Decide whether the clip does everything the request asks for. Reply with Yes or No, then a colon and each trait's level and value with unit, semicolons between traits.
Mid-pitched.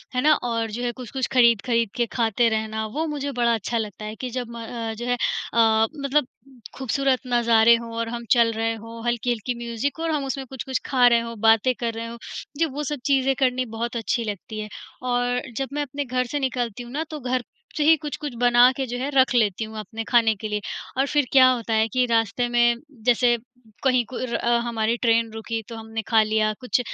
No: high, 240 Hz